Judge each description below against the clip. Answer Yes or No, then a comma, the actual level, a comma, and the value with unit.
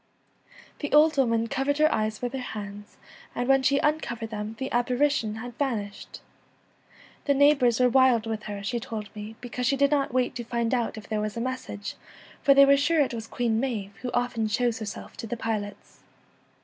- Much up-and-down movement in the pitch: No, average, 3.6 semitones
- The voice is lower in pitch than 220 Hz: No, high, 240 Hz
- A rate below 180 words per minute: No, fast, 205 wpm